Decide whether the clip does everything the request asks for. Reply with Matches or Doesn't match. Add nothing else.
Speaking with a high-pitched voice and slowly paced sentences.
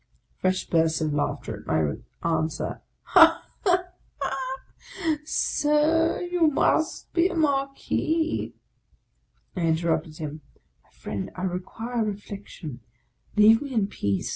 Matches